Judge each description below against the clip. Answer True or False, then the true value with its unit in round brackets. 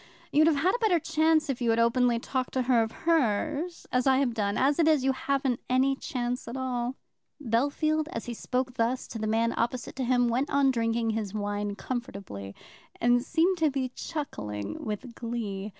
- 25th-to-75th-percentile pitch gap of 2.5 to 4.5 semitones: True (3.6 semitones)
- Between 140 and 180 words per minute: False (200 wpm)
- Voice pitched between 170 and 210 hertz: False (250 Hz)